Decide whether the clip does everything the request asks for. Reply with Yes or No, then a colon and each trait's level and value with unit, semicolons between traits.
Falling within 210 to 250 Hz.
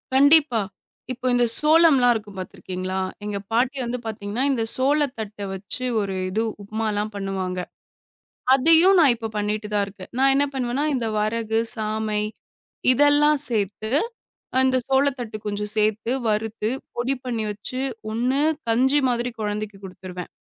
Yes: high, 225 Hz